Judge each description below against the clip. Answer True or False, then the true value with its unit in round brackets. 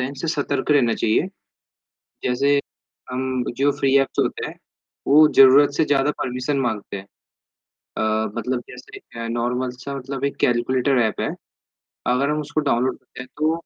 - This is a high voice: False (130 Hz)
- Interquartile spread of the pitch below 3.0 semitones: True (2.4 semitones)